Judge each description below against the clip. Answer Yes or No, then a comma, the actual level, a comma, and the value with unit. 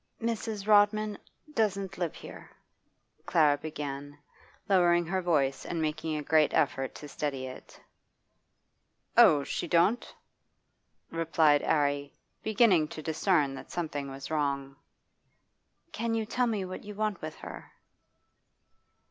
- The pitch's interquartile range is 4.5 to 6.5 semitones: Yes, wide, 5.6 semitones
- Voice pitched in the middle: Yes, medium, 160 Hz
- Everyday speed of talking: No, slow, 120 wpm